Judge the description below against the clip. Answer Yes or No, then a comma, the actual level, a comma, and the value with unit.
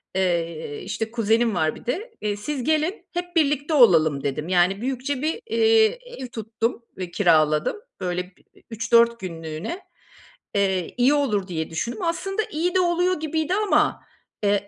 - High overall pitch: Yes, high, 230 Hz